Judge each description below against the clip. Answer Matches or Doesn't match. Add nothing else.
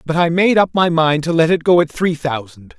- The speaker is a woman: Doesn't match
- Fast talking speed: Matches